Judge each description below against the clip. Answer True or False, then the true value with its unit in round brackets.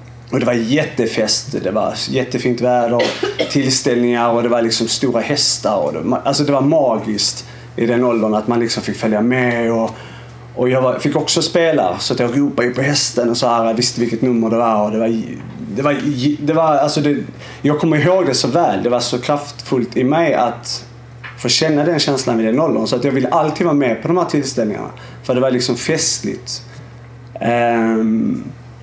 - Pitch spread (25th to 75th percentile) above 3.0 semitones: False (2.7 semitones)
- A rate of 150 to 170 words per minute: False (185 wpm)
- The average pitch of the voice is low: True (120 Hz)